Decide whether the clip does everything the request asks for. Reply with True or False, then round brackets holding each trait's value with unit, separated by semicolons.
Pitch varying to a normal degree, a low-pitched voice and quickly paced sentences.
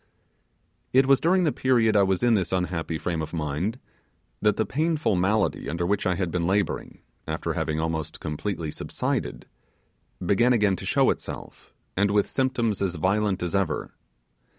False (4.5 semitones; 100 Hz; 165 wpm)